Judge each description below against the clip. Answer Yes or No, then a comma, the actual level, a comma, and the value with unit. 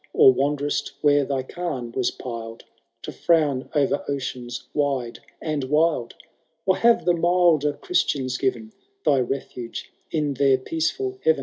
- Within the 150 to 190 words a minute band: No, slow, 135 wpm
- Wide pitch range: No, average, 4.1 semitones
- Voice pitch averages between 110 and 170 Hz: Yes, medium, 140 Hz